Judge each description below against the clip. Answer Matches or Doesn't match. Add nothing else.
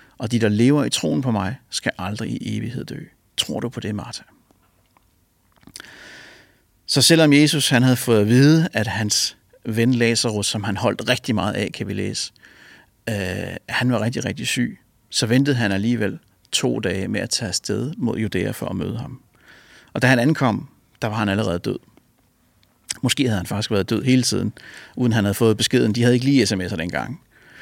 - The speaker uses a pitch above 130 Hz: Doesn't match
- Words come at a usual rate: Matches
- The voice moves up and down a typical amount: Matches